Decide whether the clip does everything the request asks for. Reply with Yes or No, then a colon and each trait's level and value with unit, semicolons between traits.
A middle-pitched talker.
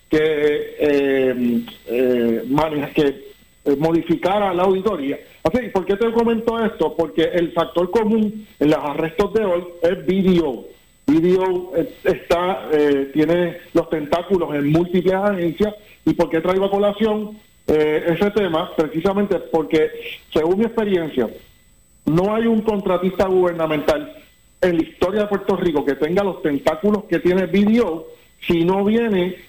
Yes: medium, 180 Hz